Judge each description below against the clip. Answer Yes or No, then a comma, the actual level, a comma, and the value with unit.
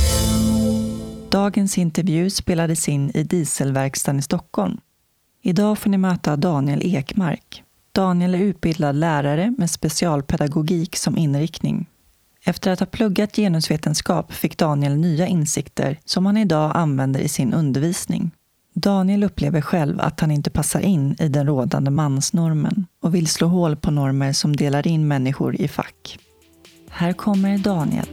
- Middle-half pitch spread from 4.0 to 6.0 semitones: Yes, average, 4.3 semitones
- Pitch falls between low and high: Yes, medium, 165 Hz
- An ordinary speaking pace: Yes, average, 140 wpm